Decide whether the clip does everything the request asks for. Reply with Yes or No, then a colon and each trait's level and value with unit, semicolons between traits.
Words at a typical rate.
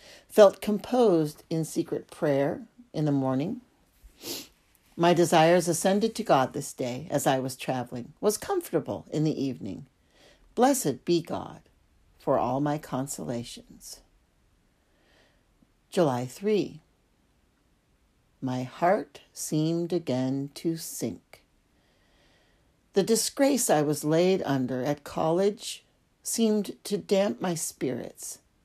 No: slow, 110 wpm